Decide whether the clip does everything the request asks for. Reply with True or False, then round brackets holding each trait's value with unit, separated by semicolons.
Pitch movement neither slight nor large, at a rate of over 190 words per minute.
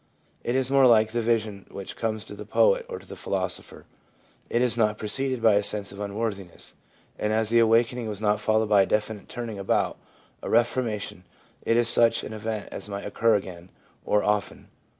False (2.2 semitones; 200 wpm)